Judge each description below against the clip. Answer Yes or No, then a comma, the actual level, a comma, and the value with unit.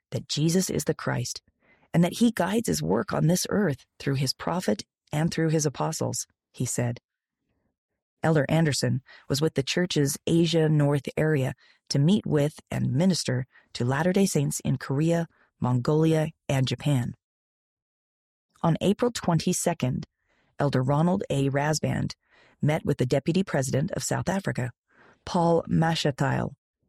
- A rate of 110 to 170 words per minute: Yes, average, 140 wpm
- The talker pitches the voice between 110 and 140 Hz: No, medium, 150 Hz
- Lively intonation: No, average, 4.2 semitones